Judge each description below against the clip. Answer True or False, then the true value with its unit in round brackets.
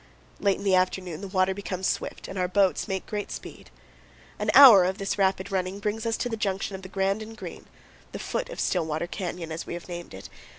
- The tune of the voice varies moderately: False (1.7 semitones)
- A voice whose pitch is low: False (190 Hz)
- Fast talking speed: True (225 wpm)